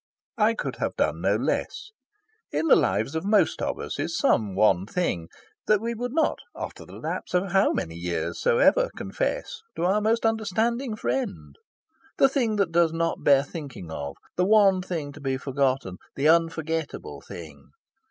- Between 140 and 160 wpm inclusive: No, average, 170 wpm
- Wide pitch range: Yes, wide, 8.5 semitones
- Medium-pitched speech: Yes, medium, 170 Hz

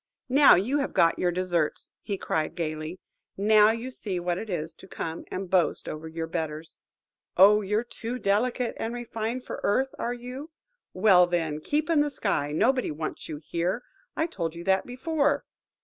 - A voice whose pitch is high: Yes, high, 200 Hz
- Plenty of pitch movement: Yes, wide, 6.8 semitones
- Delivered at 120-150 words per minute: No, average, 175 wpm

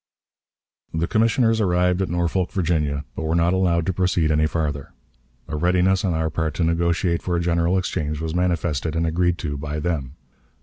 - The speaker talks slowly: No, average, 180 wpm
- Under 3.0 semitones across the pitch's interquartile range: Yes, narrow, 2.4 semitones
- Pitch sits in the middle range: No, very low, 85 Hz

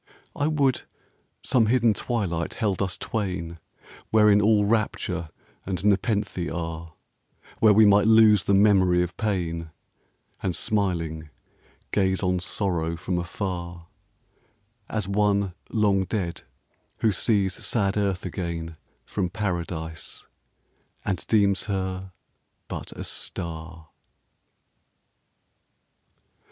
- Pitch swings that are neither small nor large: Yes, average, 3.4 semitones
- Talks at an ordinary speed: No, slow, 105 wpm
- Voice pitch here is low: Yes, very low, 95 Hz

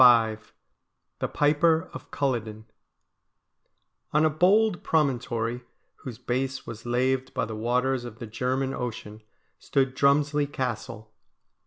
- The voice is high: No, low, 130 Hz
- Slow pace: Yes, slow, 125 wpm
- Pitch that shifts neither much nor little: Yes, average, 3.5 semitones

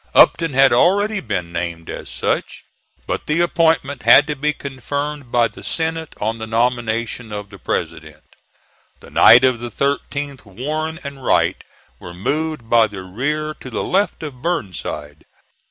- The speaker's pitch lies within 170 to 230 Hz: No, low, 130 Hz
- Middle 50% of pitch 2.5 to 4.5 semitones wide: No, wide, 5.4 semitones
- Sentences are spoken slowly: No, average, 155 wpm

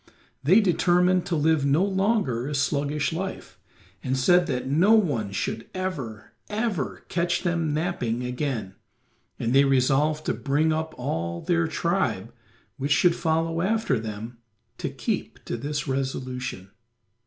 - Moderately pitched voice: Yes, medium, 150 Hz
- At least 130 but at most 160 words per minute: Yes, average, 140 wpm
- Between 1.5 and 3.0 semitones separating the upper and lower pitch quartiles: No, wide, 5.5 semitones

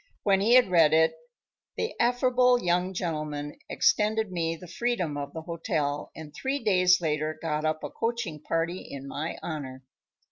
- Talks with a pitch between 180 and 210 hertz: No, medium, 170 Hz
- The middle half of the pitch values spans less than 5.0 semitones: No, wide, 5.4 semitones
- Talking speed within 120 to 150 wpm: No, average, 165 wpm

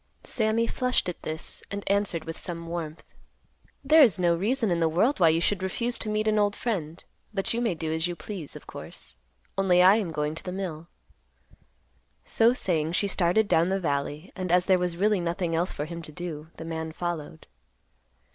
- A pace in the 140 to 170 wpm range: No, fast, 205 wpm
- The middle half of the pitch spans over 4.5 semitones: No, average, 3.9 semitones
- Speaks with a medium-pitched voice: Yes, medium, 180 Hz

